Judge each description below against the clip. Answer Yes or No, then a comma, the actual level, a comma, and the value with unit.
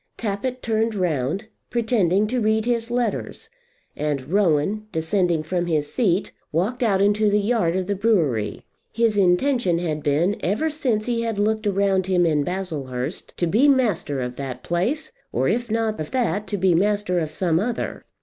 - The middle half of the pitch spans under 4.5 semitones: No, average, 5.1 semitones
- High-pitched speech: Yes, high, 200 Hz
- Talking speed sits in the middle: Yes, average, 170 wpm